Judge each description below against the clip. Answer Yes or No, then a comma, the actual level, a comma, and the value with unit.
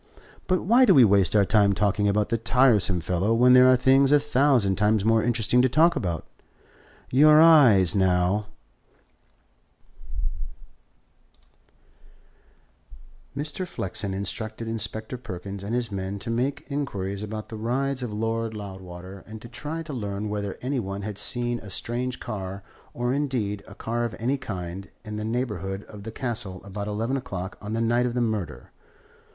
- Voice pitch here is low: Yes, low, 110 Hz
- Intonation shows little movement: No, average, 4.1 semitones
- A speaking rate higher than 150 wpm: Yes, average, 165 wpm